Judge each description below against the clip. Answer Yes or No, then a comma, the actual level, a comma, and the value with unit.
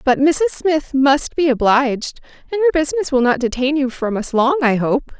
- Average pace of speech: Yes, average, 195 wpm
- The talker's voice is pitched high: Yes, very high, 275 Hz